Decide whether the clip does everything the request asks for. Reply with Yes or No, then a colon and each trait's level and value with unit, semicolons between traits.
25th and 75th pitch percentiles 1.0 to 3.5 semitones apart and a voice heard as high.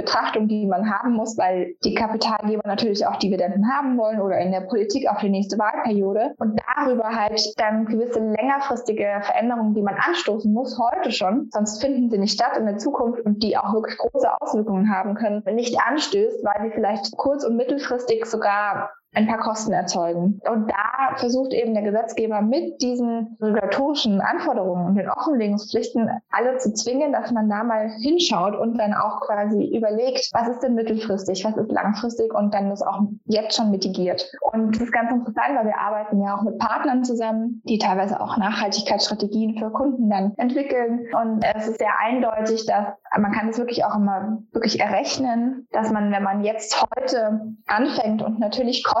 Yes: narrow, 2.5 semitones; high, 220 Hz